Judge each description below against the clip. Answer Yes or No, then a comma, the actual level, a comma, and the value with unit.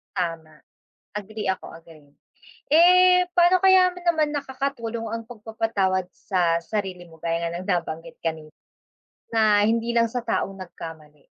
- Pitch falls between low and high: No, high, 210 Hz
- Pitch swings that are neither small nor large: No, wide, 6.6 semitones